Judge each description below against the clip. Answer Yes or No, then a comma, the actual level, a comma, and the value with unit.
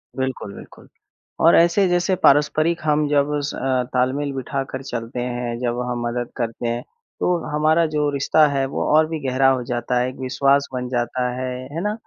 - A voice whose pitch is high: No, low, 135 Hz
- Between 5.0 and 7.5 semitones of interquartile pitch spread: No, average, 3.3 semitones